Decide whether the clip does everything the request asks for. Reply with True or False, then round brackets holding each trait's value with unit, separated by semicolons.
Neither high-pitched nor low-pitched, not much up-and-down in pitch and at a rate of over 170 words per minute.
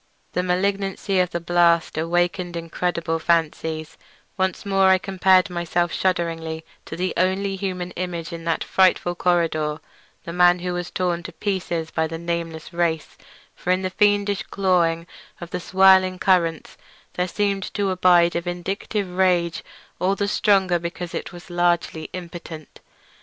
False (175 Hz; 1.8 semitones; 150 wpm)